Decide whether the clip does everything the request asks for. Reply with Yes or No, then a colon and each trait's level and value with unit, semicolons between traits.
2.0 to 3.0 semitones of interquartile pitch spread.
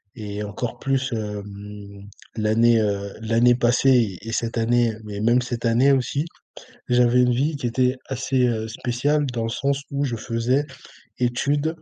Yes: average, 2.7 semitones